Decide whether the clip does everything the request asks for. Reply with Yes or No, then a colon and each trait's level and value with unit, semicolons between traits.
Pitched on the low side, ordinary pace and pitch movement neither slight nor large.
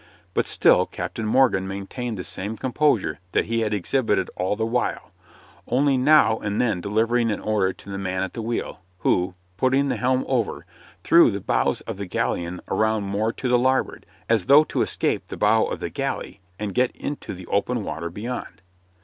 Yes: low, 110 Hz; average, 190 wpm; average, 4.4 semitones